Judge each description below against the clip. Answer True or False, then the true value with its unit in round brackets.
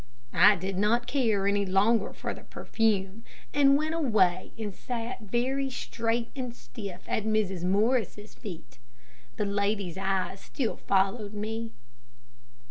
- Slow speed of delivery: True (130 wpm)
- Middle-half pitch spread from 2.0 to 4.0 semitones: True (3.4 semitones)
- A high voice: True (210 Hz)